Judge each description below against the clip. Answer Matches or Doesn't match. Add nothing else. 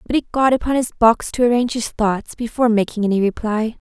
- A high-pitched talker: Matches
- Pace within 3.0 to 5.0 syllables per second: Doesn't match